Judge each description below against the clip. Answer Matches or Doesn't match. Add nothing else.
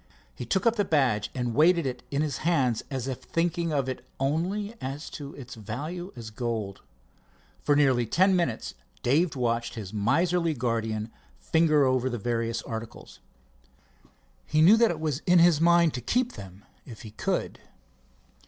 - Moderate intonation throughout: Doesn't match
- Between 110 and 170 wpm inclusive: Matches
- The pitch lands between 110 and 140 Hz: Matches